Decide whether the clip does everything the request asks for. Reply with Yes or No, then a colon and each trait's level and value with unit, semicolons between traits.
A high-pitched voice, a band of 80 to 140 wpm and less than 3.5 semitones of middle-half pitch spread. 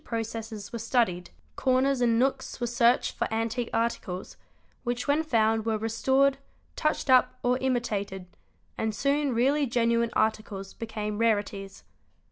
Yes: high, 230 Hz; slow, 135 wpm; average, 2.8 semitones